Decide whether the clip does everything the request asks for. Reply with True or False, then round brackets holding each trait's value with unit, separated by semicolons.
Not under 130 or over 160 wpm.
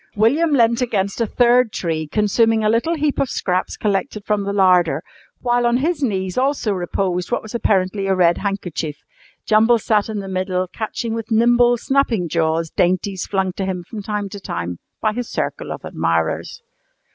False (180 wpm)